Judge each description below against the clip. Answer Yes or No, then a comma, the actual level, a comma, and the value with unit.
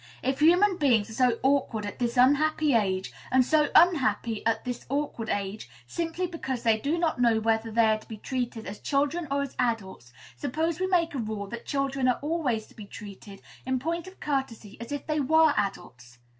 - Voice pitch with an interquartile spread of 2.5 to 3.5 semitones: No, wide, 5.5 semitones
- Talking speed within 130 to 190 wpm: No, average, 200 wpm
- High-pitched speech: Yes, very high, 255 Hz